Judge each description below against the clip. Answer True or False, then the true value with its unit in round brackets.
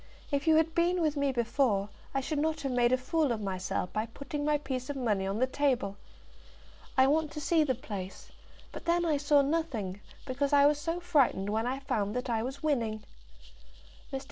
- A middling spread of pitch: True (4.7 semitones)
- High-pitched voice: True (270 Hz)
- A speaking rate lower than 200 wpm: False (205 wpm)